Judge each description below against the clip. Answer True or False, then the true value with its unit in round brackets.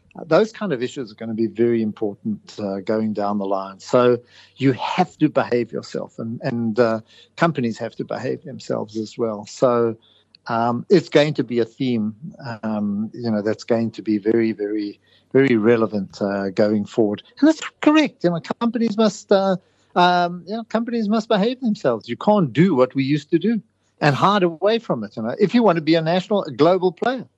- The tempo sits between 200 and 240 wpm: True (205 wpm)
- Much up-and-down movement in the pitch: True (8.8 semitones)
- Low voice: True (125 Hz)